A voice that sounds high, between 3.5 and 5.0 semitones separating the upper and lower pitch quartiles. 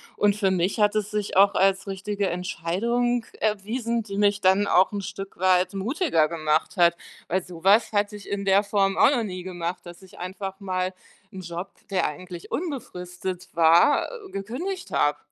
No: high, 195 Hz; narrow, 2.4 semitones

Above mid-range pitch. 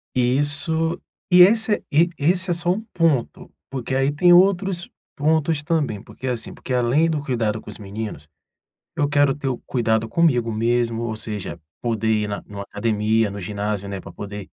No: low, 125 Hz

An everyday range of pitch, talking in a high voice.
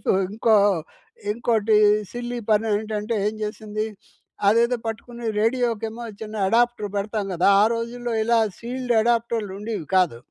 No: narrow, 2.0 semitones; high, 225 Hz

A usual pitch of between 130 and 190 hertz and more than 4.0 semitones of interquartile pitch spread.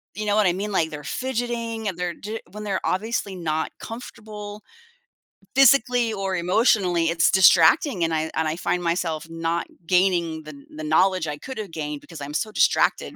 Yes: medium, 185 Hz; average, 4.7 semitones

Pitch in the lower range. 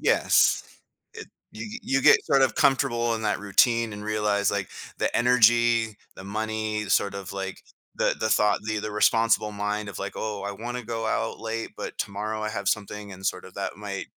Yes: low, 110 Hz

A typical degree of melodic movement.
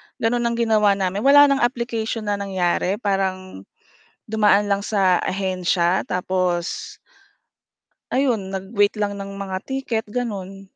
Yes: average, 3.0 semitones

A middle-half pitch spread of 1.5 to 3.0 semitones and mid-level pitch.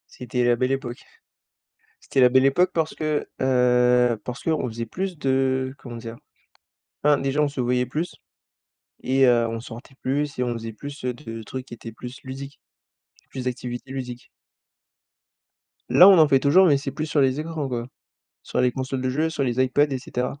No: narrow, 2.6 semitones; low, 130 Hz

